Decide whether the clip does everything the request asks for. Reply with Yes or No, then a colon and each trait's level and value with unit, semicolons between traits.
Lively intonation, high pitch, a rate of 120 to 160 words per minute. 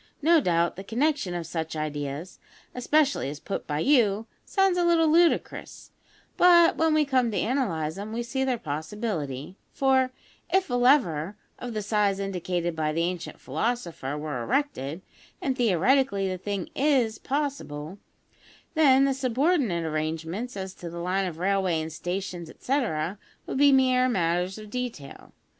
Yes: wide, 7.9 semitones; high, 200 Hz; average, 155 wpm